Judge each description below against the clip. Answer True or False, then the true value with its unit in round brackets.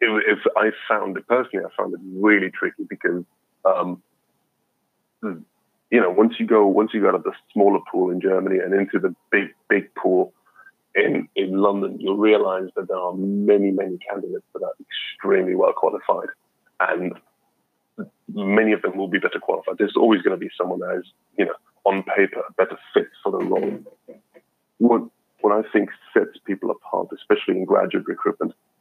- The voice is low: True (105 Hz)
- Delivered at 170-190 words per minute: True (175 wpm)